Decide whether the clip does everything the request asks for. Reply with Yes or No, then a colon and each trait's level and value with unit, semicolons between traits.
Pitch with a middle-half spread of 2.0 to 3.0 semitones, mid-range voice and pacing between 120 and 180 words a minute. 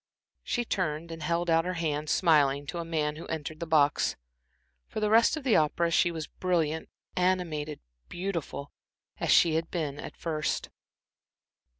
Yes: narrow, 2.4 semitones; medium, 165 Hz; average, 165 wpm